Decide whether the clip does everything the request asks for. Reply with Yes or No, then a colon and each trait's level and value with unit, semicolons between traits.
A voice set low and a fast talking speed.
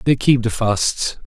No: low, 120 Hz; average, 190 wpm